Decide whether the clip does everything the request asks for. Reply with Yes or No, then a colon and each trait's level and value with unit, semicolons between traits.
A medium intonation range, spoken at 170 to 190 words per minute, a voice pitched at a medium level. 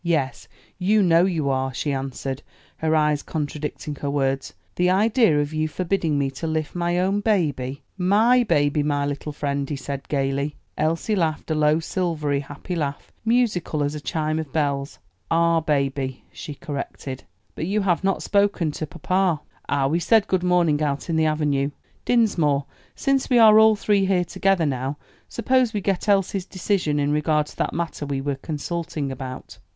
Yes: average, 4.5 semitones; average, 175 wpm; medium, 155 Hz